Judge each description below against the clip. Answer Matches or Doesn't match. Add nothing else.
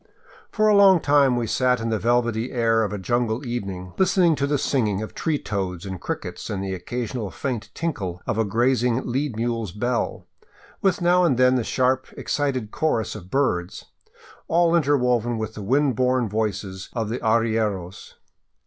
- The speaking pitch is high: Doesn't match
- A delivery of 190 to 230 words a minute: Doesn't match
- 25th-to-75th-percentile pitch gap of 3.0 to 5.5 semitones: Matches